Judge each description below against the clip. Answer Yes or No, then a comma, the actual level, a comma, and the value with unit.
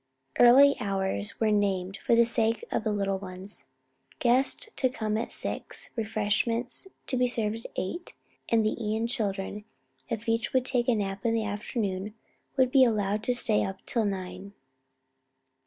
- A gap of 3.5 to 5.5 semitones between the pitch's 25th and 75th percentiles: No, average, 3.0 semitones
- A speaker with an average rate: Yes, average, 165 wpm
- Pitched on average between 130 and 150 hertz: No, high, 220 Hz